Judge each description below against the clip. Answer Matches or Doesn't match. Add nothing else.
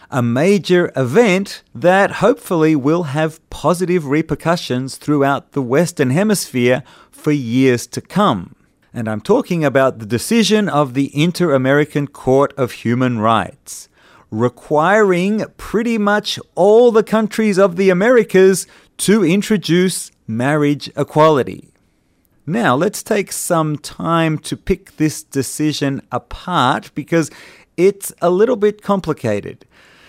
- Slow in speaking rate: Matches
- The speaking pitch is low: Doesn't match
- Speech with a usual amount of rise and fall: Doesn't match